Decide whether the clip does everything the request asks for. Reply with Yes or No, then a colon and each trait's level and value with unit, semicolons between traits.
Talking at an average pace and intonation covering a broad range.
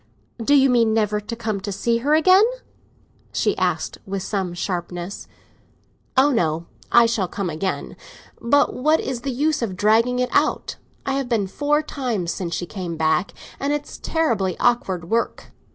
Yes: average, 170 wpm; wide, 6.0 semitones